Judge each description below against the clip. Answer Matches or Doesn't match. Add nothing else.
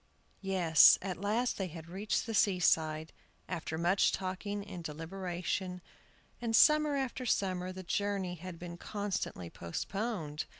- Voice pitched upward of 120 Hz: Matches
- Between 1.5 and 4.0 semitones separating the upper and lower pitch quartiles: Matches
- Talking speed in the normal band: Doesn't match